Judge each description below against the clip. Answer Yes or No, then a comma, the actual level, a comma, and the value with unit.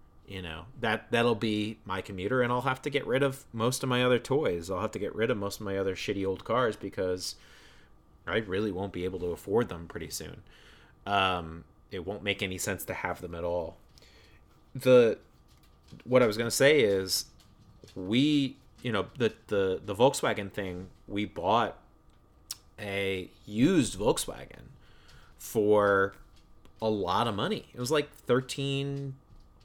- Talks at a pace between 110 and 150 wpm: No, average, 170 wpm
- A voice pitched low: Yes, low, 100 Hz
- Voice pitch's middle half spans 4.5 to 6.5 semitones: Yes, average, 4.8 semitones